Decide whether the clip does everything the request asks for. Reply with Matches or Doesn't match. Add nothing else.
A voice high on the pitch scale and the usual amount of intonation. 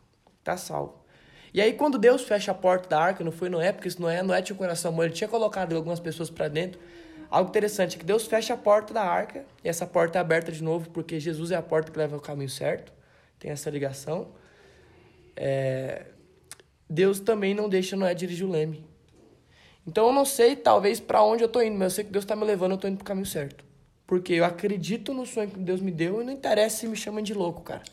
Doesn't match